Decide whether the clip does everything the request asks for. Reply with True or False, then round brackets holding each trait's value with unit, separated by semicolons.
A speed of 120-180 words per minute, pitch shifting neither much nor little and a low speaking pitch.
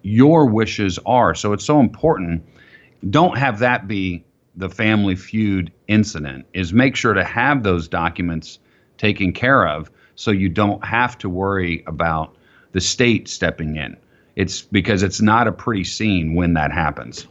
True (160 wpm; 4.5 semitones; 95 Hz)